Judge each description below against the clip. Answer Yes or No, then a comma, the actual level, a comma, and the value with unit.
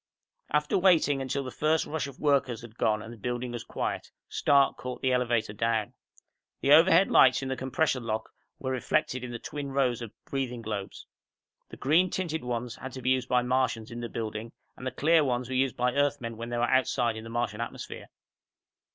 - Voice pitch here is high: No, low, 125 Hz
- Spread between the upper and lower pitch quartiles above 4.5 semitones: No, average, 2.9 semitones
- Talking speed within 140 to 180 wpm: No, fast, 205 wpm